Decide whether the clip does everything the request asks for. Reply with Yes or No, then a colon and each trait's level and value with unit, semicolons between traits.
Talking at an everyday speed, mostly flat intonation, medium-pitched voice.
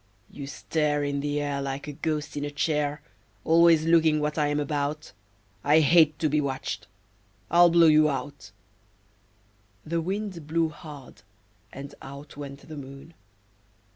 Yes: average, 150 wpm; narrow, 2.0 semitones; medium, 150 Hz